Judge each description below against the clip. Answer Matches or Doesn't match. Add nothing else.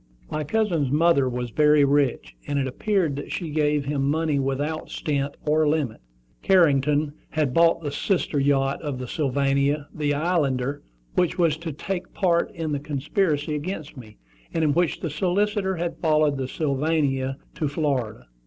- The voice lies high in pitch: Doesn't match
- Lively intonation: Doesn't match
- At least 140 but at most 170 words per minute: Matches